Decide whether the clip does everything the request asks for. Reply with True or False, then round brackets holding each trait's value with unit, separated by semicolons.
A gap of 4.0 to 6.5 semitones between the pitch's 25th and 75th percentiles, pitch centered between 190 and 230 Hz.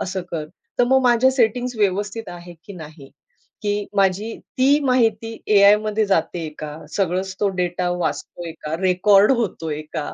True (4.3 semitones; 200 Hz)